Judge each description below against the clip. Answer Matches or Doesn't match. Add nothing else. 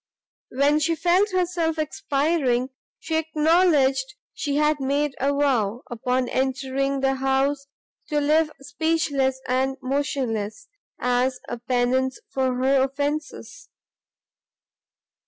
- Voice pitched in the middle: Doesn't match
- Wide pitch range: Doesn't match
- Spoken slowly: Matches